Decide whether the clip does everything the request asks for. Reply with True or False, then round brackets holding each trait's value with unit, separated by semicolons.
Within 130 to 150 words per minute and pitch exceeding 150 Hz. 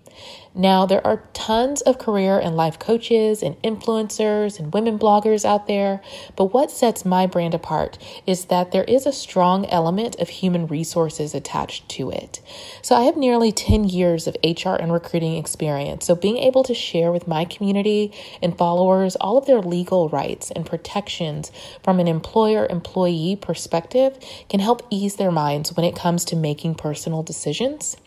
False (170 wpm; 185 Hz)